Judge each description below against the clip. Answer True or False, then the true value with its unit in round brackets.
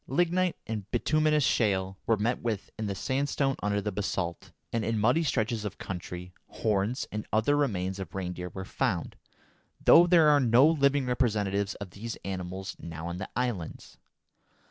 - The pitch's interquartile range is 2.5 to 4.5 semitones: False (5.6 semitones)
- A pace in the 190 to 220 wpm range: False (165 wpm)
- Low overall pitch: True (110 Hz)